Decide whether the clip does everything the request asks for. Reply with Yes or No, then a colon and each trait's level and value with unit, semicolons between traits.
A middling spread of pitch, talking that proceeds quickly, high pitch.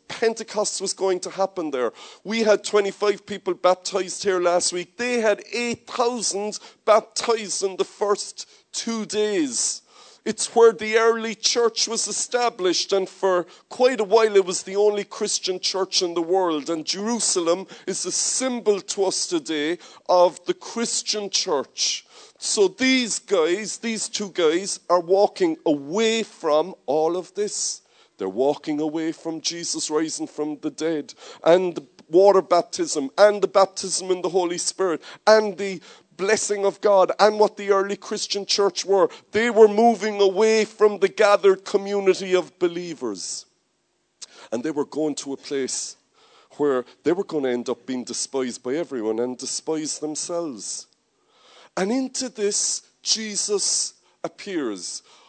No: average, 4.1 semitones; average, 150 wpm; high, 195 Hz